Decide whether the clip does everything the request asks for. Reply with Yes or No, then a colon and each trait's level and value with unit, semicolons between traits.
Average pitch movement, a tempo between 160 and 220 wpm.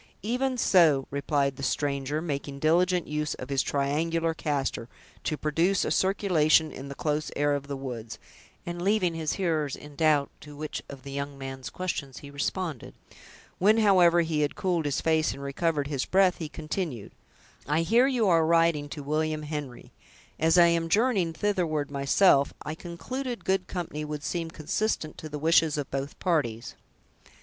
Yes: average, 3.5 semitones; average, 170 wpm